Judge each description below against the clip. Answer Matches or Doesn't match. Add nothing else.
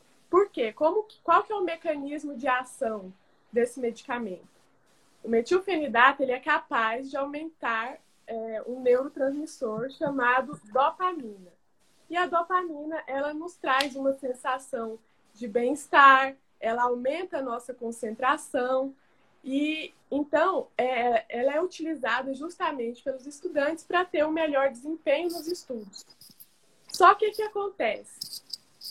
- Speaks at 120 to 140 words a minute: Matches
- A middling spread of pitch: Matches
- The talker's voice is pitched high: Matches